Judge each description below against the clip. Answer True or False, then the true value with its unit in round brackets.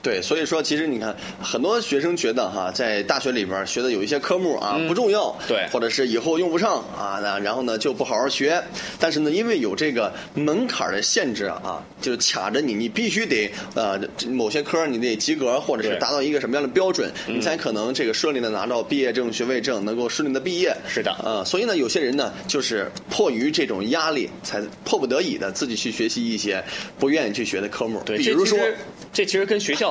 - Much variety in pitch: True (9.0 semitones)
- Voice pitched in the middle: True (165 Hz)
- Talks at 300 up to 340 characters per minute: True (335 characters per minute)